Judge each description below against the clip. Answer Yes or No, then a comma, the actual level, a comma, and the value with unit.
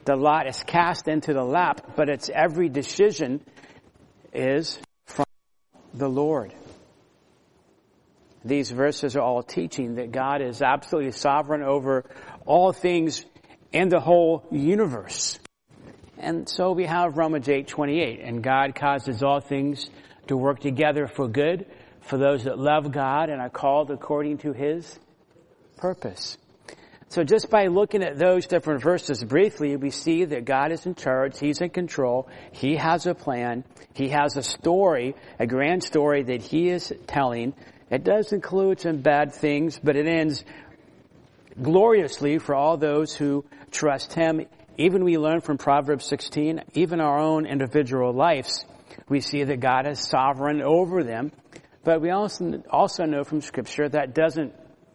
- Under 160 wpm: Yes, average, 150 wpm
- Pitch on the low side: No, medium, 145 Hz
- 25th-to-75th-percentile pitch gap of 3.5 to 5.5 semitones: No, average, 3.0 semitones